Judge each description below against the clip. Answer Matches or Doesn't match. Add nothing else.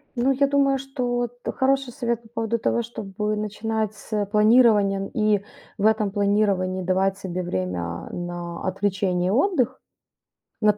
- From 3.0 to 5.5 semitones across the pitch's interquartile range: Matches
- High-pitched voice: Matches